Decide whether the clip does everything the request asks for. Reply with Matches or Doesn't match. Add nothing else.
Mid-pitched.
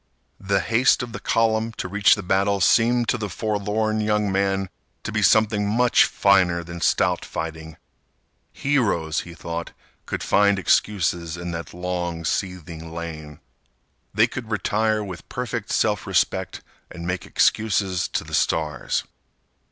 Doesn't match